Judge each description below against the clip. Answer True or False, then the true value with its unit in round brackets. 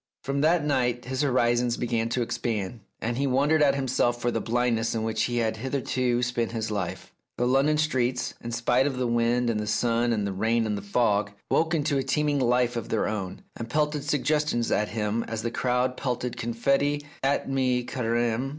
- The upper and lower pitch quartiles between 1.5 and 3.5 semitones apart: True (2.7 semitones)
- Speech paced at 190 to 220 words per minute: True (200 wpm)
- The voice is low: True (120 Hz)